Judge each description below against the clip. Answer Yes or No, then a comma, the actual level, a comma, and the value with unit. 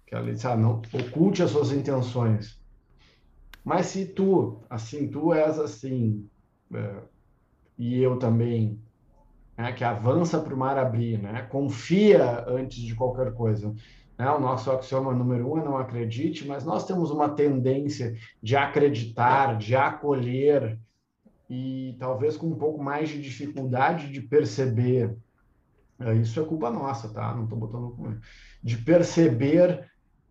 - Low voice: Yes, low, 130 Hz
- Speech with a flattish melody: No, average, 3.8 semitones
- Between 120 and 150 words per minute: Yes, average, 145 wpm